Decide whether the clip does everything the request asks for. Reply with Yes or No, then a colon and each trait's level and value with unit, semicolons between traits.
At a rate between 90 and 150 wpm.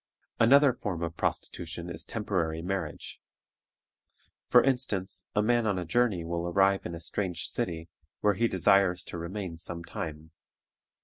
Yes: average, 145 wpm